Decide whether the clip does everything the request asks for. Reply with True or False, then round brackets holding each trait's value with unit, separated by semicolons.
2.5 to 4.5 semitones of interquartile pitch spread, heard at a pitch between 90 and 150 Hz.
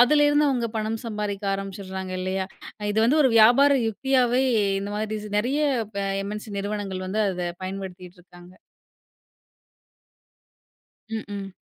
False (4.0 semitones; 210 Hz)